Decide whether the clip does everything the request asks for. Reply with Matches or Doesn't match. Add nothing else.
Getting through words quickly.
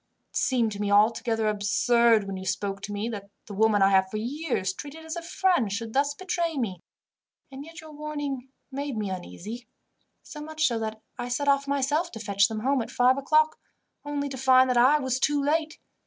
Matches